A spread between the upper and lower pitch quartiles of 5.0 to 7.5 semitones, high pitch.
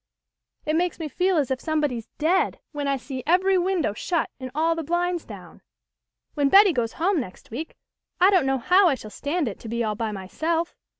Yes: wide, 5.4 semitones; very high, 310 Hz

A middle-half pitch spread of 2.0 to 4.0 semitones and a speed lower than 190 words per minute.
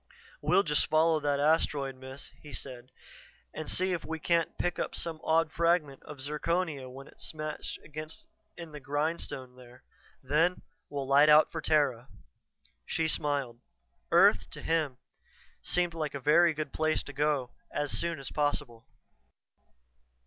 Yes: average, 2.9 semitones; average, 150 wpm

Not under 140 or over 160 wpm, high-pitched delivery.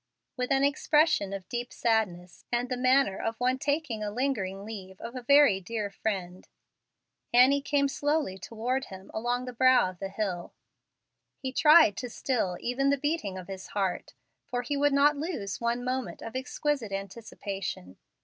No: average, 170 wpm; high, 240 Hz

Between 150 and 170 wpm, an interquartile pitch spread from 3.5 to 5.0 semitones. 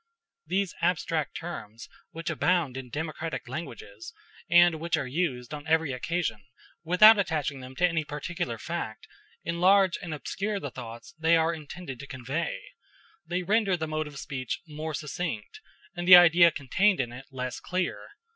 Yes: average, 155 wpm; average, 4.5 semitones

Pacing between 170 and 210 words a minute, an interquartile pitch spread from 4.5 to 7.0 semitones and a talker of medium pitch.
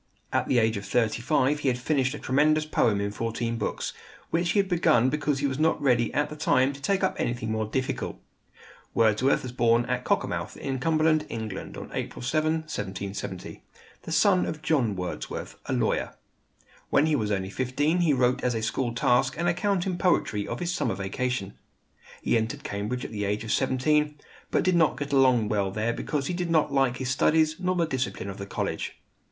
No: fast, 205 wpm; wide, 5.4 semitones; low, 130 Hz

